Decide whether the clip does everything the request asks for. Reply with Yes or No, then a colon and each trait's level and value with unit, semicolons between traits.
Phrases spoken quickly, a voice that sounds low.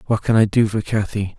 Yes: fast, 260 wpm; low, 105 Hz